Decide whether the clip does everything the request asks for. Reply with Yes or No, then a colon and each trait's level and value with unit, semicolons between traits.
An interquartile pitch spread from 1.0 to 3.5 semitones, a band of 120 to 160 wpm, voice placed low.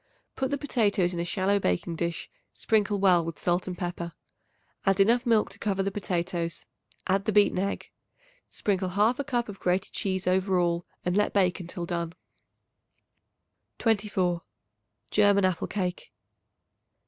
No: average, 2.7 semitones; average, 150 wpm; high, 190 Hz